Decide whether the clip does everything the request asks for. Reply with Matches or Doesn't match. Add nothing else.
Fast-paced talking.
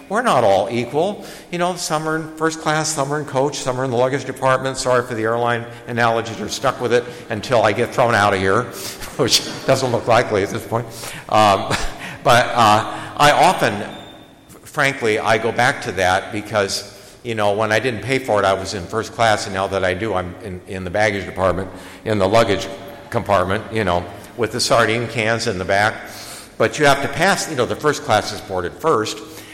Matches